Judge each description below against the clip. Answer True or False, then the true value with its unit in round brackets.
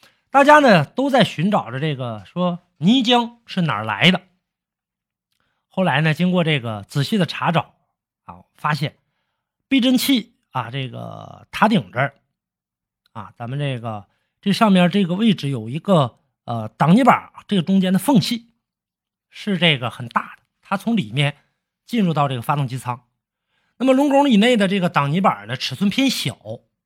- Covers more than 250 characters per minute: False (235 characters per minute)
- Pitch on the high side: False (175 Hz)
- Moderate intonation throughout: False (7.5 semitones)